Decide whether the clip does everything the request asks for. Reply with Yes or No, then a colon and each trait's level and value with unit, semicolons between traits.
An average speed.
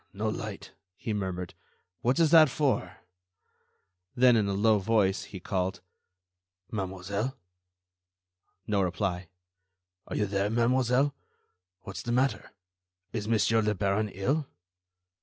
No: slow, 120 wpm